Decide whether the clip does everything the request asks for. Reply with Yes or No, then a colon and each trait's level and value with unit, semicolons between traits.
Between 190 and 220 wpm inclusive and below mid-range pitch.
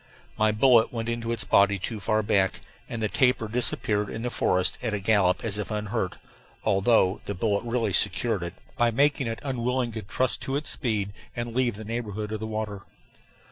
Yes: average, 195 wpm; low, 110 Hz